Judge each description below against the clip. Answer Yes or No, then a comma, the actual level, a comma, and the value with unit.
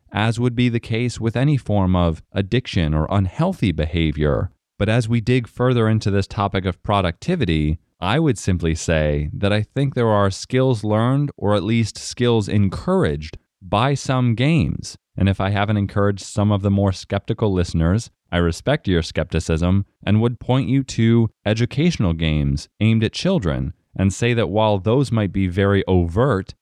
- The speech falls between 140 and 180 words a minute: Yes, average, 170 wpm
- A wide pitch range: No, average, 4.3 semitones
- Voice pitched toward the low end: Yes, low, 105 Hz